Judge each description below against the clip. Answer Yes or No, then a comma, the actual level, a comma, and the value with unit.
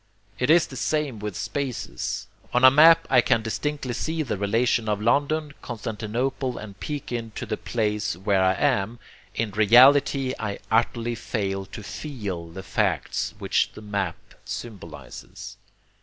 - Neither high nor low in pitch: No, low, 115 Hz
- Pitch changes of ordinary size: Yes, average, 4.6 semitones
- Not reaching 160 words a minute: Yes, average, 145 wpm